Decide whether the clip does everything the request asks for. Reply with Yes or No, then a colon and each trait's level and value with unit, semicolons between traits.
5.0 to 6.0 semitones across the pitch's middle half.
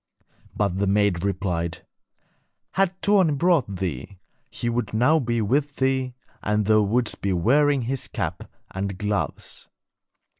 Yes: wide, 5.5 semitones